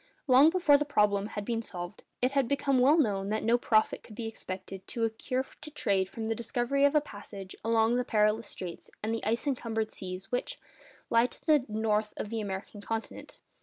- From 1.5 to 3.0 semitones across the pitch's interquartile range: No, average, 3.4 semitones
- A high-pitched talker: Yes, high, 225 Hz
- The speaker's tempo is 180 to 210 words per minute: Yes, fast, 205 wpm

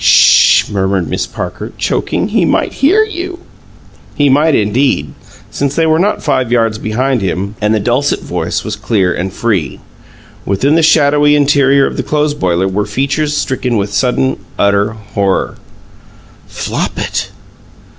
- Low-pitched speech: Yes, low, 125 Hz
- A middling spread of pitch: No, wide, 6.4 semitones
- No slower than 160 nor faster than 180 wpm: No, average, 145 wpm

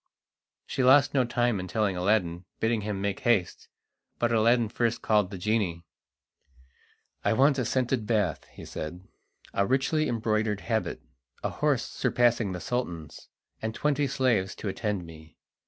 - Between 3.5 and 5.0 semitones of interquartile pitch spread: Yes, average, 4.1 semitones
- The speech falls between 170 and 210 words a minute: No, average, 150 wpm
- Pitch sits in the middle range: No, low, 110 Hz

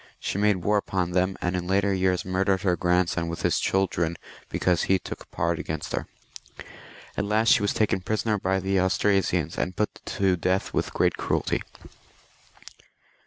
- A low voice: Yes, very low, 95 Hz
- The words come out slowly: No, average, 165 wpm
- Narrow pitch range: Yes, narrow, 1.8 semitones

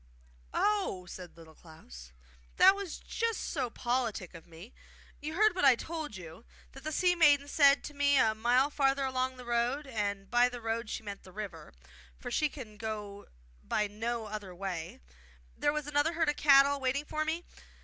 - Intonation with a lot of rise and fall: Yes, wide, 6.1 semitones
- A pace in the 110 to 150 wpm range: No, average, 185 wpm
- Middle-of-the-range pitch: No, very high, 250 Hz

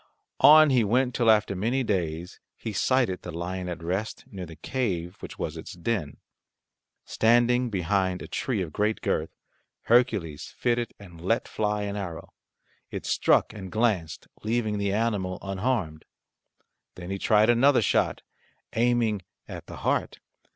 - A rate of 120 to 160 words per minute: Yes, average, 150 wpm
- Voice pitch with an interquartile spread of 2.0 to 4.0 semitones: No, average, 4.4 semitones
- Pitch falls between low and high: No, low, 105 Hz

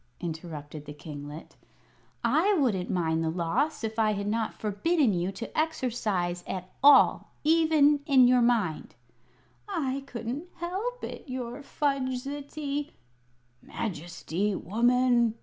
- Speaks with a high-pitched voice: Yes, high, 235 Hz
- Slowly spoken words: Yes, slow, 120 wpm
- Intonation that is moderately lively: No, wide, 8.2 semitones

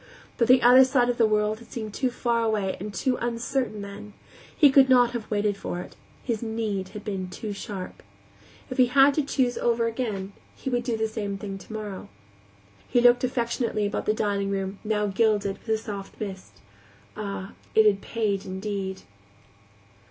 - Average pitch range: Yes, average, 3.1 semitones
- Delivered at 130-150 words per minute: No, average, 180 wpm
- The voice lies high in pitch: Yes, high, 215 Hz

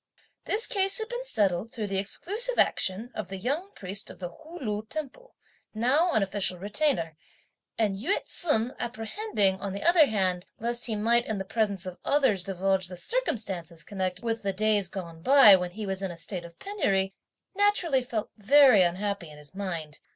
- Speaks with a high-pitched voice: Yes, high, 210 Hz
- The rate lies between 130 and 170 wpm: No, average, 185 wpm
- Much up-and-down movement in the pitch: Yes, wide, 6.3 semitones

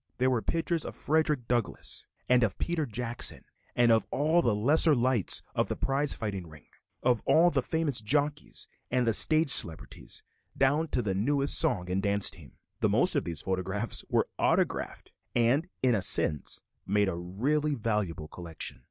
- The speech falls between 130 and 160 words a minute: No, average, 170 wpm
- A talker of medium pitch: No, low, 120 Hz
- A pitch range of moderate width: No, wide, 6.4 semitones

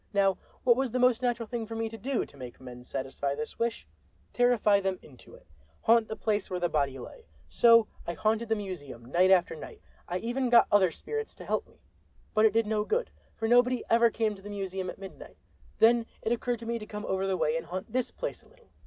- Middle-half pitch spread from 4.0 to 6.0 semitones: Yes, average, 4.3 semitones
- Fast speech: Yes, fast, 235 wpm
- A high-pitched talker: Yes, high, 215 Hz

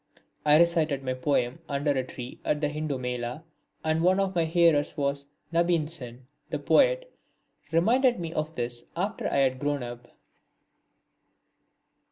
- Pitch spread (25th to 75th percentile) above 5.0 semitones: No, average, 4.7 semitones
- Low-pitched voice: No, medium, 150 Hz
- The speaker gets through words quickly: No, average, 155 wpm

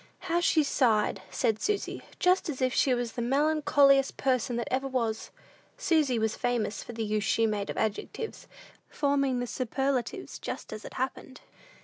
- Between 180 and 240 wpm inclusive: No, average, 165 wpm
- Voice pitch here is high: Yes, very high, 255 Hz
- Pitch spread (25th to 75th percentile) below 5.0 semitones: Yes, average, 3.8 semitones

